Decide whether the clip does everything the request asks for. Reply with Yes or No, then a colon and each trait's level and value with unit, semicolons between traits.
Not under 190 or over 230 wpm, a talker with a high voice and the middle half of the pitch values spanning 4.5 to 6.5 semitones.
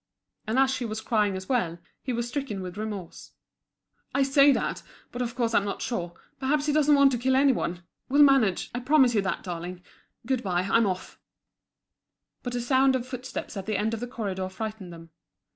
Yes: fast, 205 wpm; high, 235 Hz; average, 5.3 semitones